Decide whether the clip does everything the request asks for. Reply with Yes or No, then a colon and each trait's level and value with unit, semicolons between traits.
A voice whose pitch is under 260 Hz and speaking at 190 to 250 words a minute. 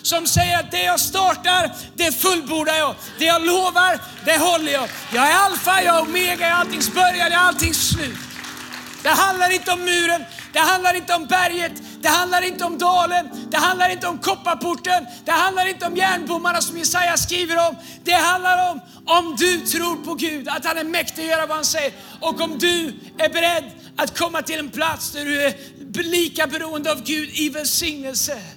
No: very high, 335 Hz; fast, 195 wpm